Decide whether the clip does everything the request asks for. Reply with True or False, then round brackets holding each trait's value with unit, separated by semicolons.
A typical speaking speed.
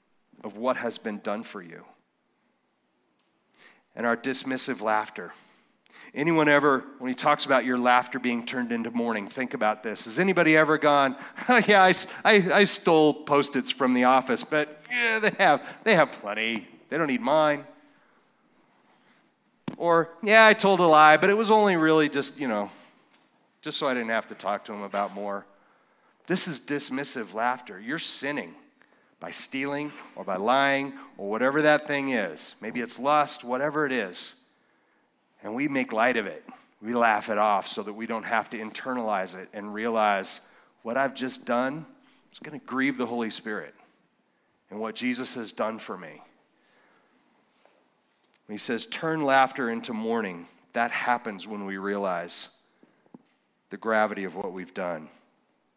True (165 wpm)